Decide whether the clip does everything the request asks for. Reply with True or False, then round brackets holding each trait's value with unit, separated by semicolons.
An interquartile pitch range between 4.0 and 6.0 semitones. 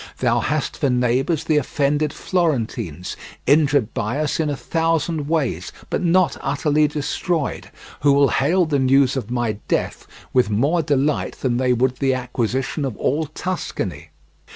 False (3.6 semitones)